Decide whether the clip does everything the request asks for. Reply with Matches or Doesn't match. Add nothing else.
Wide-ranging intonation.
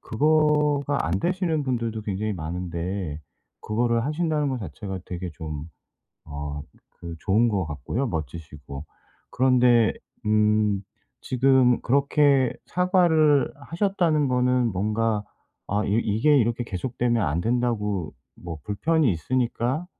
Matches